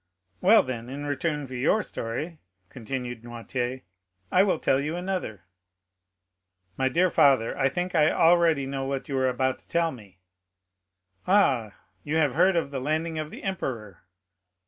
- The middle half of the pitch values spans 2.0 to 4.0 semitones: No, average, 4.8 semitones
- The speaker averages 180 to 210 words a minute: No, average, 160 wpm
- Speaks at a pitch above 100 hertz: Yes, medium, 140 Hz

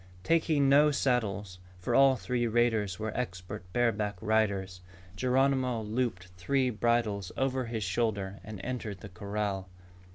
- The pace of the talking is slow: Yes, slow, 130 wpm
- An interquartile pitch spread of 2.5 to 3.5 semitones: No, average, 4.2 semitones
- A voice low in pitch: Yes, low, 110 Hz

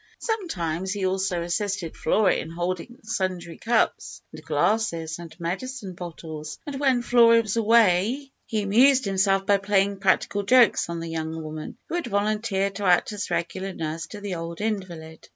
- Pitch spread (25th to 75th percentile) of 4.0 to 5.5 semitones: Yes, average, 4.4 semitones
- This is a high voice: Yes, high, 195 Hz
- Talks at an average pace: Yes, average, 165 wpm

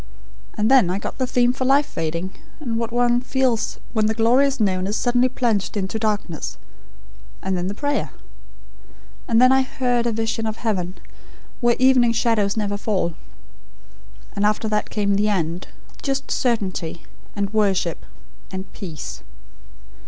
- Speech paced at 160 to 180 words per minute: No, average, 150 wpm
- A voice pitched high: Yes, high, 220 Hz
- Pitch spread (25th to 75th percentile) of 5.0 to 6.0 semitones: No, average, 3.9 semitones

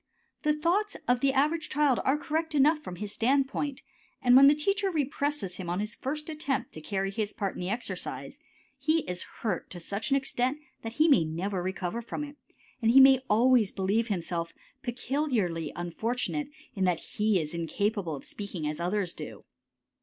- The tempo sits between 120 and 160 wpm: No, average, 185 wpm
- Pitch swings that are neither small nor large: No, wide, 7.2 semitones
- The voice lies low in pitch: No, high, 235 Hz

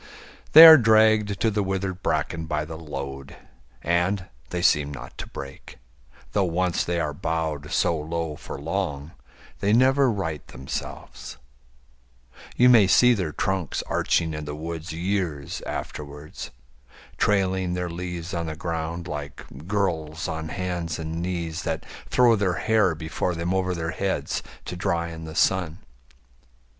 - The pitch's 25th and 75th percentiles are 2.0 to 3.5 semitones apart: Yes, average, 3.2 semitones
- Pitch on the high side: No, very low, 85 Hz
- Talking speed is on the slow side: No, average, 150 wpm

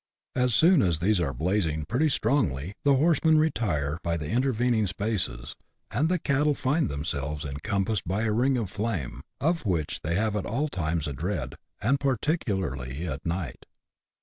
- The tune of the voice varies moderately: No, wide, 8.8 semitones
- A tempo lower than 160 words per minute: No, average, 170 wpm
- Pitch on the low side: Yes, low, 100 Hz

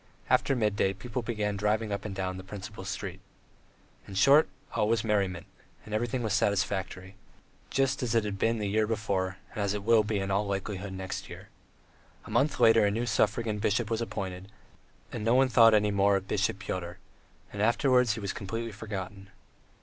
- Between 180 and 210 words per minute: Yes, average, 185 wpm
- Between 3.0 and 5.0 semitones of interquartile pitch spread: No, narrow, 2.6 semitones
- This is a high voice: No, low, 105 Hz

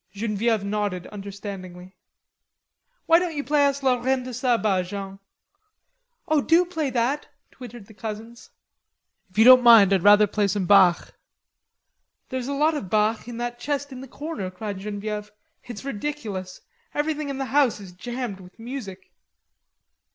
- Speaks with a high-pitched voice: Yes, high, 225 Hz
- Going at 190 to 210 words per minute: No, average, 155 wpm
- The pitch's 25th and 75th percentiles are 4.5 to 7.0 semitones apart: Yes, average, 5.1 semitones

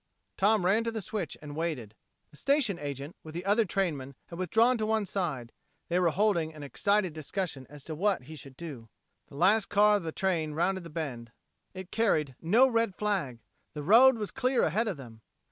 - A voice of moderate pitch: Yes, medium, 175 Hz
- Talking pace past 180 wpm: Yes, average, 200 wpm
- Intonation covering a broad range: Yes, wide, 5.9 semitones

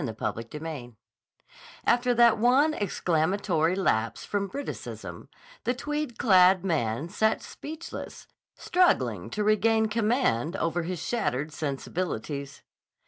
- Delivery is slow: Yes, slow, 105 wpm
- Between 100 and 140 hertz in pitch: No, high, 190 Hz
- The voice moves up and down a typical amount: No, wide, 6.9 semitones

